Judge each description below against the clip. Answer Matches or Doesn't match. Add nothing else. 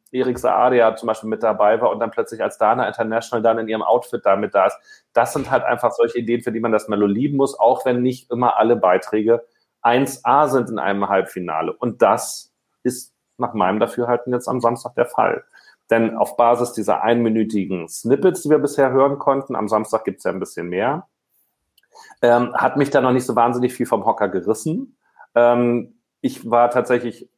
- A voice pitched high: Doesn't match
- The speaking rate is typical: Doesn't match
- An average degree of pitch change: Doesn't match